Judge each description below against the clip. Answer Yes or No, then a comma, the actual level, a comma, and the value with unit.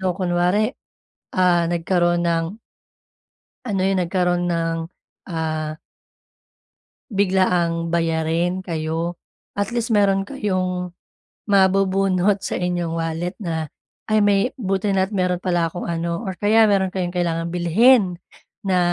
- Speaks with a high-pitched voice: No, medium, 180 Hz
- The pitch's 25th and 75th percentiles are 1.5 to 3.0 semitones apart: Yes, narrow, 2.5 semitones